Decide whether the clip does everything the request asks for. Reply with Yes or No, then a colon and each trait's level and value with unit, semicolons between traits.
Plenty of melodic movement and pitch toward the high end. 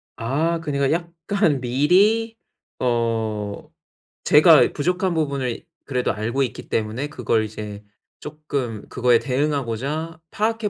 No: wide, 5.9 semitones; medium, 140 Hz